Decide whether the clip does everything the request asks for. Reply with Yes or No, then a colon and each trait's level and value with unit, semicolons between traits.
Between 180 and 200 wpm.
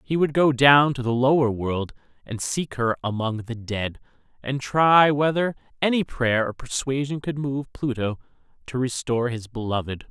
No: average, 165 wpm